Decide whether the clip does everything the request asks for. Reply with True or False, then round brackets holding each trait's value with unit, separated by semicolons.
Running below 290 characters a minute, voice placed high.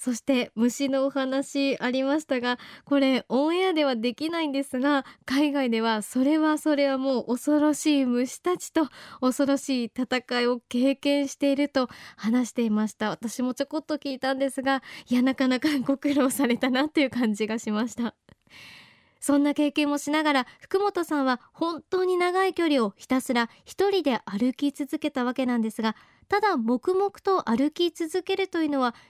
False (340 characters per minute; 270 Hz)